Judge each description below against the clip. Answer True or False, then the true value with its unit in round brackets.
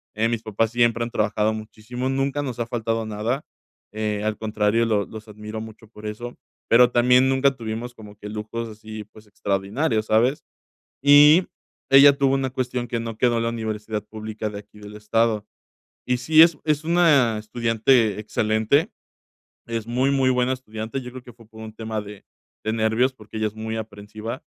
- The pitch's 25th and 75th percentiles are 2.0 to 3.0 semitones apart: True (2.6 semitones)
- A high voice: False (115 Hz)